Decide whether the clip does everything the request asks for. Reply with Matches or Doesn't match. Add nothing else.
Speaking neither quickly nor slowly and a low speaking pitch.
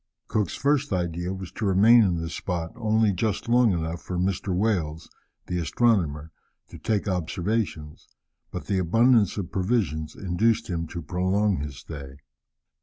Matches